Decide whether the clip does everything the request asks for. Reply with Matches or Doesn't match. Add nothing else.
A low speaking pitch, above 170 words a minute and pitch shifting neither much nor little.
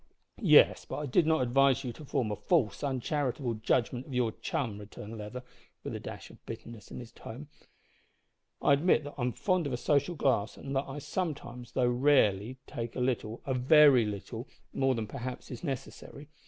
Matches